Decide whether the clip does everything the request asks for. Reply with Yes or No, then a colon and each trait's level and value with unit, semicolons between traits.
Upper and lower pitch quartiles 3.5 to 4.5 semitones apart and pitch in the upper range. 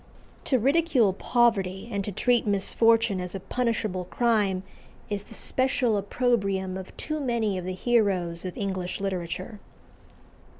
Yes: average, 4.1 semitones; high, 205 Hz